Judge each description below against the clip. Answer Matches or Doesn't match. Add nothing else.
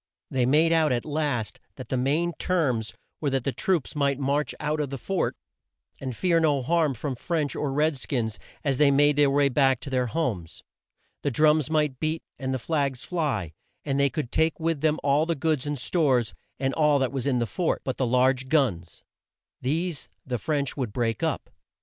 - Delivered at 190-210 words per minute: Matches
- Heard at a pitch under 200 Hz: Matches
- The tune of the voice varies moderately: Matches